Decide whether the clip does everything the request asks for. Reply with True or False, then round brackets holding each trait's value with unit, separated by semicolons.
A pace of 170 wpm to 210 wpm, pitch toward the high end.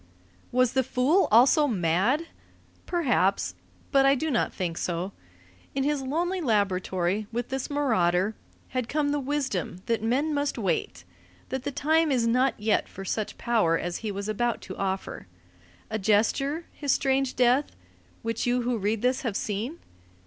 False (160 wpm; 240 Hz)